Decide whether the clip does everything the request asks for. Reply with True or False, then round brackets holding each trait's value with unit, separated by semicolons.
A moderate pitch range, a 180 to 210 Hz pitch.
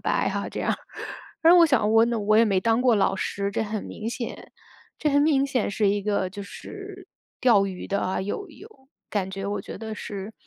False (5.0 semitones; 220 Hz)